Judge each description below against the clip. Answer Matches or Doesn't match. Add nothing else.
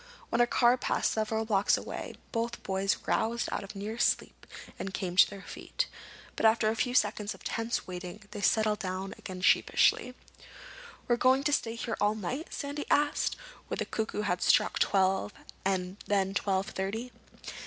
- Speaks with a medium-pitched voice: Doesn't match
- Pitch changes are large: Doesn't match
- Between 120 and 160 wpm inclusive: Doesn't match